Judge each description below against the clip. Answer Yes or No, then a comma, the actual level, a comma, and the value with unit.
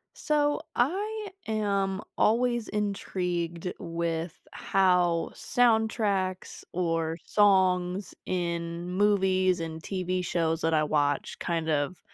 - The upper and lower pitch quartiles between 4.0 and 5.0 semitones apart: No, average, 3.6 semitones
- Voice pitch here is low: No, medium, 185 Hz